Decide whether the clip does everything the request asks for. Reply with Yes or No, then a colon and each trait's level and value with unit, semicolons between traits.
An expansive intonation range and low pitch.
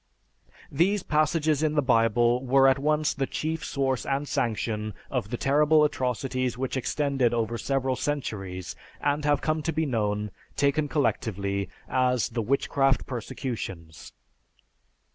No: average, 4.2 semitones; low, 130 Hz